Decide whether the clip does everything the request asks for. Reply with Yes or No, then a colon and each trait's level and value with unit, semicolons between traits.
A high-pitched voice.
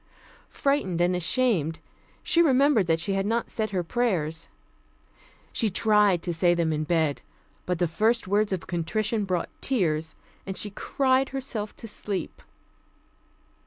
Yes: high, 195 Hz